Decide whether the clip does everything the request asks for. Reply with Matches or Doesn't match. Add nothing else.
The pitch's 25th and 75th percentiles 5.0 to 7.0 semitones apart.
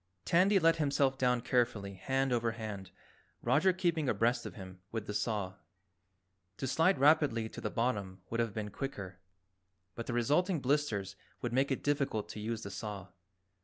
Matches